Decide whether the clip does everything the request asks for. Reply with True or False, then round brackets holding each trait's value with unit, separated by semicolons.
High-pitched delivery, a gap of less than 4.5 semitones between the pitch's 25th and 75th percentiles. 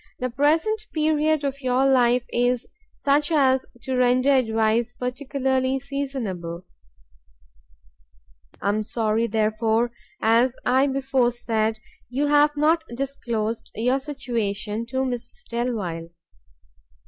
True (250 Hz; 3.5 semitones)